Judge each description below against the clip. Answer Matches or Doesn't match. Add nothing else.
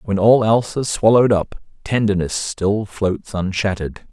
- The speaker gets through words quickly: Doesn't match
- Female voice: Doesn't match